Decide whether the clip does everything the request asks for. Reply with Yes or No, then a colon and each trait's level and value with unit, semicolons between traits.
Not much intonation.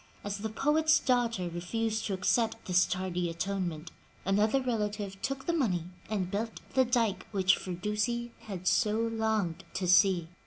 No: average, 3.7 semitones